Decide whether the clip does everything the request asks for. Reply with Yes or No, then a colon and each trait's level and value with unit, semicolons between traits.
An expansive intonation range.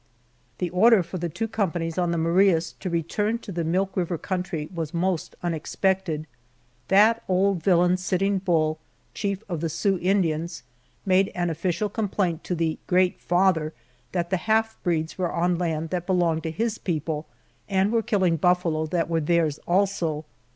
No: average, 2.7 semitones